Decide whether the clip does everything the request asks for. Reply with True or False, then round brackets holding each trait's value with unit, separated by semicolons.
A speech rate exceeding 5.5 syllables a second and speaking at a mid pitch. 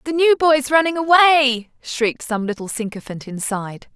False (5.9 syllables/s; 260 Hz)